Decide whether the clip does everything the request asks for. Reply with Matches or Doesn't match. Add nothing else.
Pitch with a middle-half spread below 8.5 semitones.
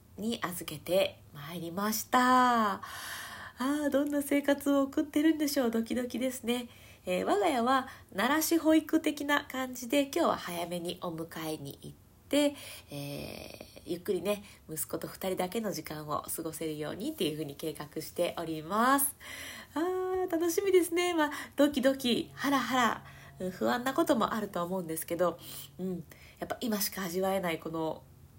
Doesn't match